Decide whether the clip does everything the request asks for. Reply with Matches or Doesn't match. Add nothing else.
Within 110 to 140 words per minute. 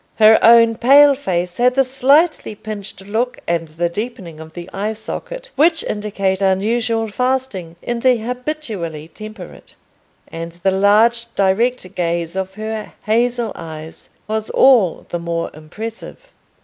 Matches